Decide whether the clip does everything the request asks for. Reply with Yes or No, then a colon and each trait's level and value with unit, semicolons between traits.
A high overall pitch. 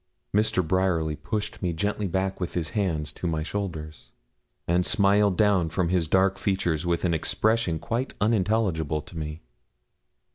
No: very low, 90 Hz